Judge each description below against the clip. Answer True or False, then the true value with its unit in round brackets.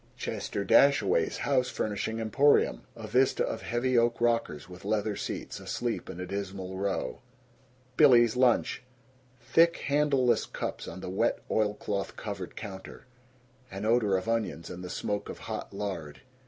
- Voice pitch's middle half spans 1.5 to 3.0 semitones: False (3.7 semitones)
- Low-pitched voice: True (110 Hz)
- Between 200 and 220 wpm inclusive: False (145 wpm)